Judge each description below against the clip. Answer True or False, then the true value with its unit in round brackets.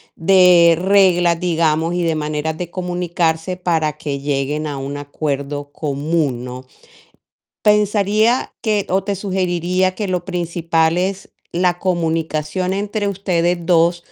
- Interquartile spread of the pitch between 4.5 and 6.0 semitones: False (3.1 semitones)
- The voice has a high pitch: False (170 Hz)